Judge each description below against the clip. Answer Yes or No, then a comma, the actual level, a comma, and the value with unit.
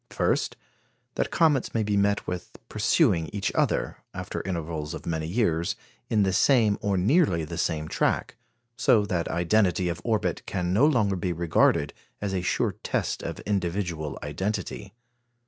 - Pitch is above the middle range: No, very low, 95 Hz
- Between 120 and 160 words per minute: Yes, average, 155 wpm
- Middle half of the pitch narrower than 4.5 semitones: Yes, average, 3.8 semitones